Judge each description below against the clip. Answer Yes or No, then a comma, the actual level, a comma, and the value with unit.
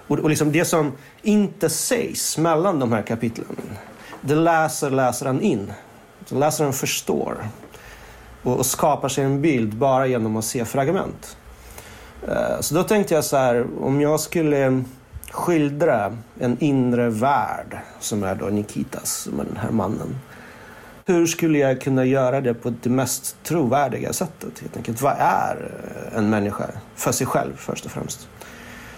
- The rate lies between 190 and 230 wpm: No, average, 145 wpm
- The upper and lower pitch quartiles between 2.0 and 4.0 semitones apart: No, average, 4.4 semitones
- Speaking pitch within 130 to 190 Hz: Yes, low, 135 Hz